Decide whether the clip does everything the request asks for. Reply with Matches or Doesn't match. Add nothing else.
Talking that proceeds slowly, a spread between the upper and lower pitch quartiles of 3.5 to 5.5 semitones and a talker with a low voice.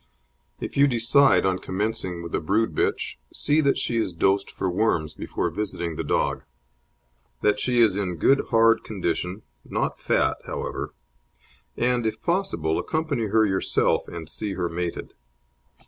Doesn't match